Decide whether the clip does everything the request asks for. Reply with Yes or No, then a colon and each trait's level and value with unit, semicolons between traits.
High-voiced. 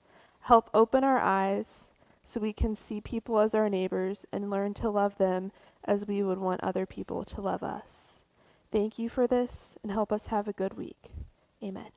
Yes: high, 210 Hz